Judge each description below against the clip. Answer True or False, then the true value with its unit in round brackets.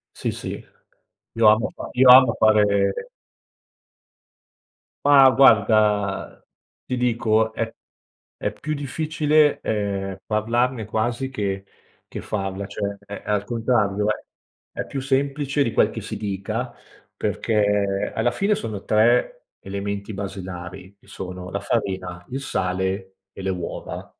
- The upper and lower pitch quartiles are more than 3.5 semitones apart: True (4.0 semitones)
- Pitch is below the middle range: True (105 Hz)